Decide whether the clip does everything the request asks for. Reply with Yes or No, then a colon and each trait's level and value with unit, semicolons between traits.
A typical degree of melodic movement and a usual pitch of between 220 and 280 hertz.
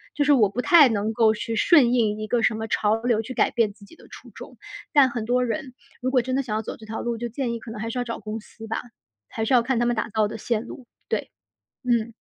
No: narrow, 2.3 semitones; high, 230 Hz